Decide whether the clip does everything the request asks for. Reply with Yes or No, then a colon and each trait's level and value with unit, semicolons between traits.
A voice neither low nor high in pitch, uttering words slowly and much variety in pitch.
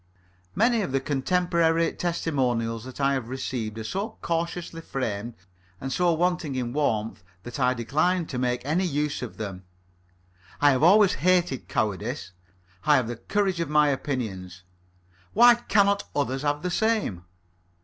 No: medium, 145 Hz; average, 150 wpm; wide, 6.3 semitones